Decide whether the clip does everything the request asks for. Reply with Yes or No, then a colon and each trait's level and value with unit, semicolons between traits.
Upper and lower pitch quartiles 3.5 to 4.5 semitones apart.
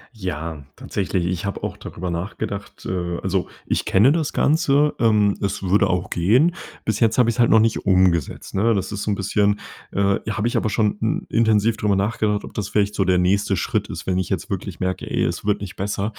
No: average, 2.8 semitones